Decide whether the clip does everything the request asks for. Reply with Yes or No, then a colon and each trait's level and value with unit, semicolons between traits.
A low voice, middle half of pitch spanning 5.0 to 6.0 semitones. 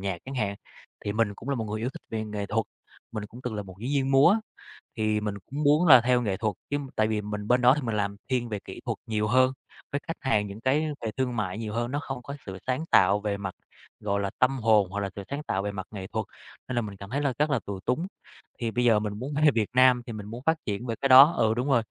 No: low, 115 Hz; average, 3.9 semitones